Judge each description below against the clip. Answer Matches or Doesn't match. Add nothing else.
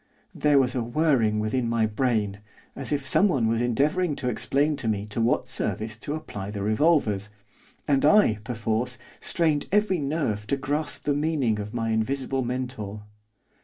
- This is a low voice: Matches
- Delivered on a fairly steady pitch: Doesn't match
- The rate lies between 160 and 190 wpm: Matches